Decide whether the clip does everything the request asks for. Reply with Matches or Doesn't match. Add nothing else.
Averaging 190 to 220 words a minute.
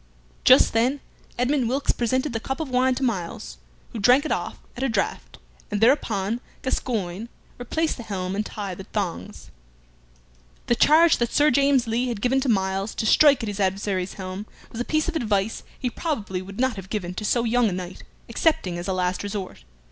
Matches